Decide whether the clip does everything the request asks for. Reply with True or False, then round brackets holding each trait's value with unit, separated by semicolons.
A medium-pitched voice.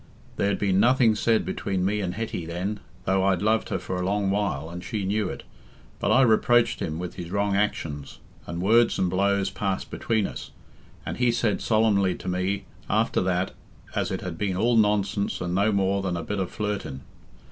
False (100 Hz)